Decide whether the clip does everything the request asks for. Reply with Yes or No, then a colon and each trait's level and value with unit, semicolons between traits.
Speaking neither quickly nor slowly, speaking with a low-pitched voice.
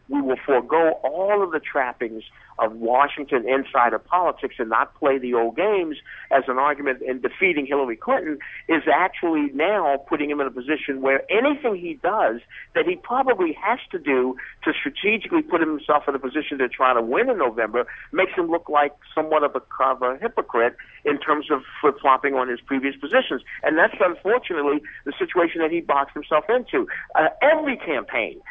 No: average, 180 wpm; medium, 155 Hz